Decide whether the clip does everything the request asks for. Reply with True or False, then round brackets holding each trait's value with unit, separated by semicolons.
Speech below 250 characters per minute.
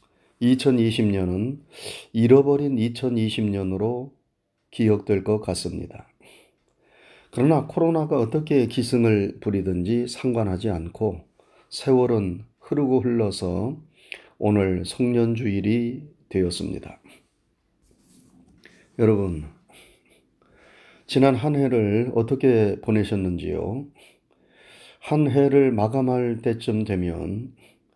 True (190 characters per minute)